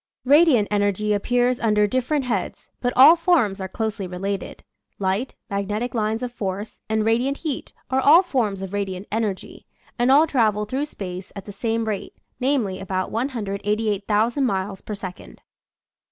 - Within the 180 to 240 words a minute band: No, average, 155 wpm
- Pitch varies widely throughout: No, average, 4.1 semitones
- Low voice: No, high, 215 Hz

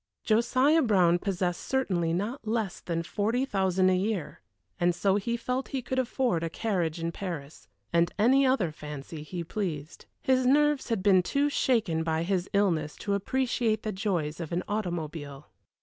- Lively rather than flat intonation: Yes, wide, 5.7 semitones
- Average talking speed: Yes, average, 165 wpm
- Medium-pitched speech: No, high, 195 Hz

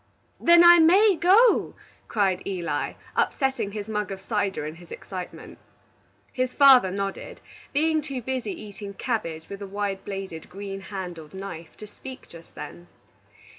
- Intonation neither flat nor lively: No, wide, 5.9 semitones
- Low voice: No, high, 200 Hz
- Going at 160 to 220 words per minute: No, average, 145 wpm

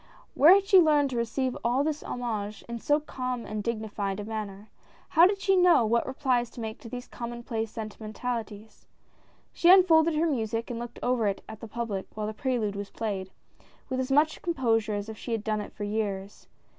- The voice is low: No, high, 235 Hz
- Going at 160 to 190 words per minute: No, fast, 205 wpm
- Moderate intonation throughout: Yes, average, 3.8 semitones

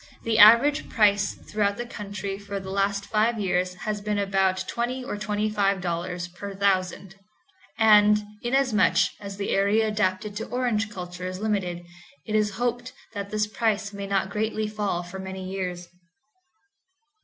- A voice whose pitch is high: Yes, high, 205 Hz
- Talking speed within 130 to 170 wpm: Yes, average, 150 wpm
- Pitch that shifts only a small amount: Yes, narrow, 2.1 semitones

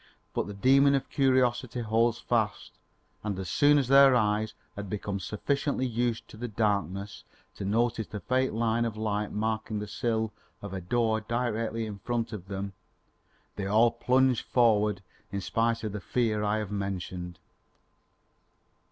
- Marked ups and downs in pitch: No, average, 2.7 semitones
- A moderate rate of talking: Yes, average, 160 wpm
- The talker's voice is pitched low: Yes, low, 110 Hz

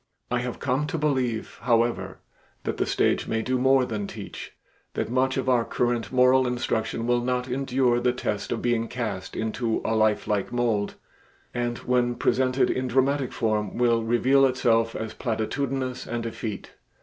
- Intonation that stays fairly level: Yes, narrow, 2.1 semitones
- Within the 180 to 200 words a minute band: No, average, 160 wpm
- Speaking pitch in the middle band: No, low, 120 Hz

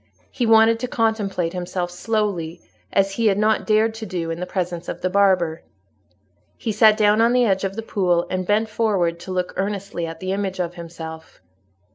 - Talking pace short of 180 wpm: No, average, 195 wpm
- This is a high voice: Yes, high, 195 Hz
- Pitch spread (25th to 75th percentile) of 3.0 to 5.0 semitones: Yes, average, 3.6 semitones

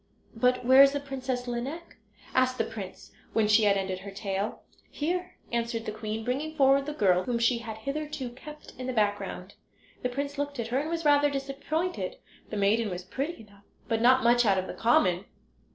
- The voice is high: Yes, high, 245 Hz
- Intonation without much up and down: No, average, 4.5 semitones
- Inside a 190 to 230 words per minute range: Yes, average, 200 wpm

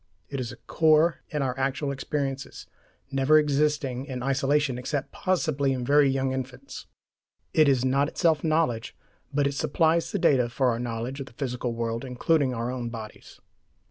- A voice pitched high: No, low, 135 Hz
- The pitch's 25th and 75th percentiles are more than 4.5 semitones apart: No, average, 2.8 semitones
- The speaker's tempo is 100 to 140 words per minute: No, average, 170 wpm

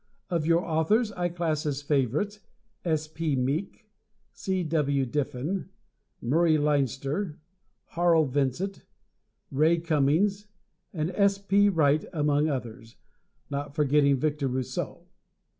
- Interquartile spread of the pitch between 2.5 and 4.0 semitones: Yes, average, 3.7 semitones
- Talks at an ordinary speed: No, slow, 110 wpm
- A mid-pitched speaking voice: Yes, medium, 155 Hz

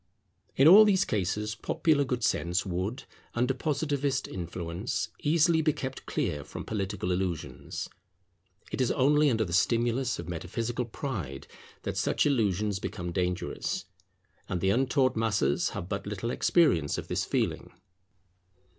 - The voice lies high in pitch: No, low, 110 Hz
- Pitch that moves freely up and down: Yes, wide, 6.9 semitones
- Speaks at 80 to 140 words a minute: Yes, slow, 135 wpm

